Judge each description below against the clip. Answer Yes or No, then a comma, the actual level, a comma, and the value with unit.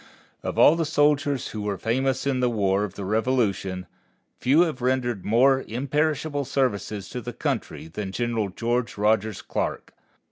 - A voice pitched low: Yes, low, 120 Hz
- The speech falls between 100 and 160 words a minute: Yes, average, 155 wpm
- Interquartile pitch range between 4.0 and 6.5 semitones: Yes, average, 4.4 semitones